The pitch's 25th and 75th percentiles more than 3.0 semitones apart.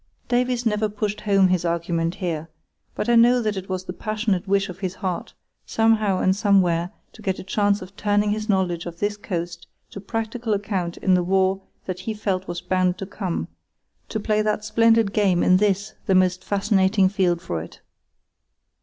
No: narrow, 2.5 semitones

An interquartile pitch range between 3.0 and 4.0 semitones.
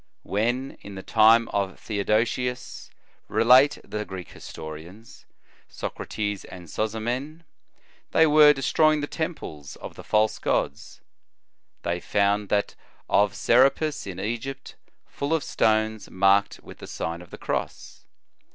No: average, 5.0 semitones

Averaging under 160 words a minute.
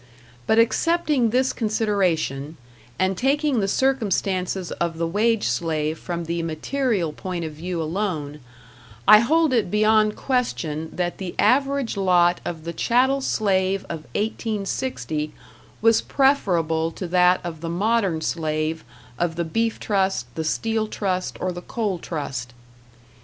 Yes: slow, 135 wpm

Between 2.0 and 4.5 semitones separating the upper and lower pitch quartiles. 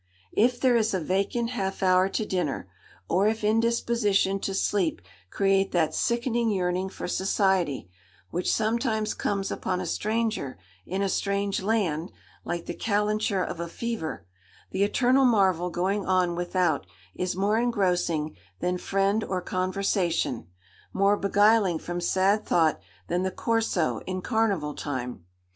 Yes: average, 3.3 semitones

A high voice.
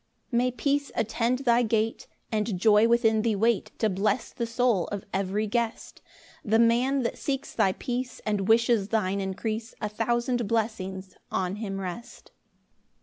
Yes: high, 225 Hz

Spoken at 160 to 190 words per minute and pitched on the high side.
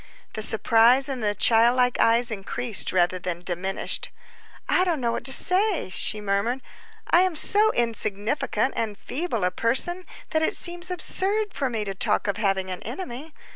Yes: average, 175 wpm; high, 235 Hz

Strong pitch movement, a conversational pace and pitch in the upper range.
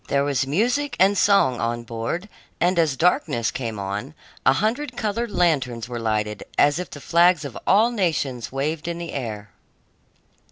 No: wide, 7.4 semitones; average, 165 wpm; medium, 145 Hz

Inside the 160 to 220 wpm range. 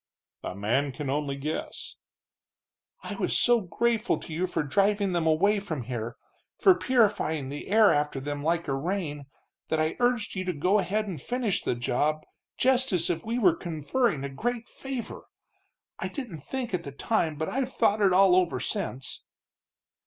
Yes: average, 175 wpm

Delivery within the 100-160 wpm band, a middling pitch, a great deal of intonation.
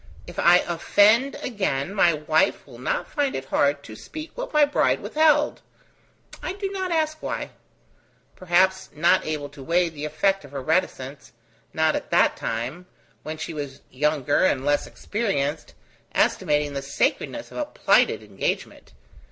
Yes: average, 155 wpm; medium, 165 Hz; wide, 6.9 semitones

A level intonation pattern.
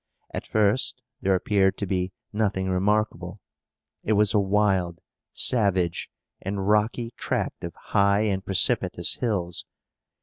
Yes: narrow, 1.9 semitones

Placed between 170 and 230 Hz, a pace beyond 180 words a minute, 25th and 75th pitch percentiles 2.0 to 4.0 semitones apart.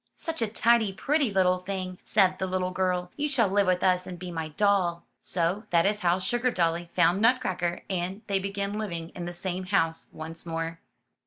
Yes: medium, 185 Hz; average, 190 wpm; average, 2.8 semitones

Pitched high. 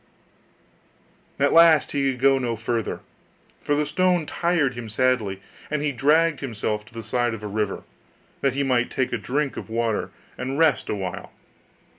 No: low, 130 Hz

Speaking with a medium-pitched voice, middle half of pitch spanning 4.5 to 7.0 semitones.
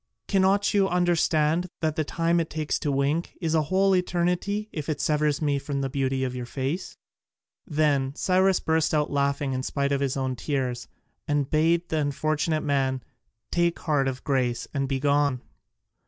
No: medium, 150 Hz; average, 3.5 semitones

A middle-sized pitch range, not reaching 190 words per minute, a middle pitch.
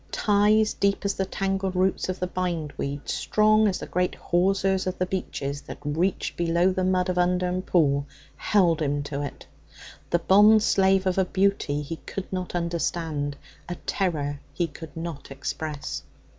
Yes: average, 3.3 semitones; average, 160 wpm; medium, 180 Hz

